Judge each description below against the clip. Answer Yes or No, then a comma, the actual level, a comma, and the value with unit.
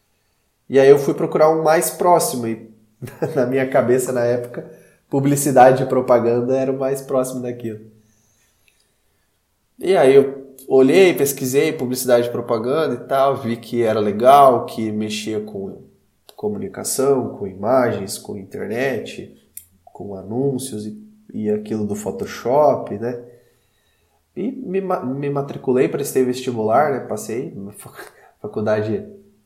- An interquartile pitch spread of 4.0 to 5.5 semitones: Yes, average, 4.4 semitones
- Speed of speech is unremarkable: Yes, average, 130 wpm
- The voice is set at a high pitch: No, low, 125 Hz